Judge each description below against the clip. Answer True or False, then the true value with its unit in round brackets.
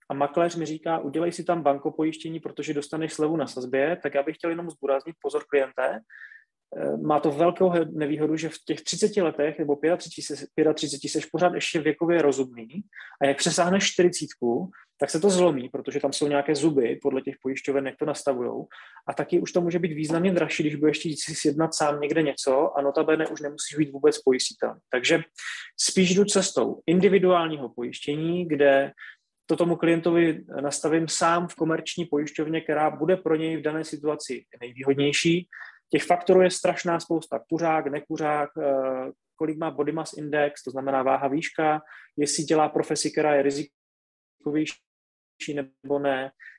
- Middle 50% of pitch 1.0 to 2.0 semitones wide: False (2.7 semitones)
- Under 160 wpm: False (165 wpm)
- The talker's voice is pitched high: False (155 Hz)